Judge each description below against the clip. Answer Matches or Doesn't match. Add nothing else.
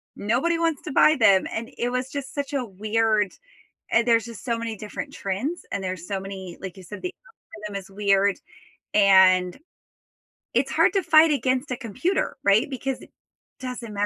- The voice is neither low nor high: Doesn't match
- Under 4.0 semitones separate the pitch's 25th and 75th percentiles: Doesn't match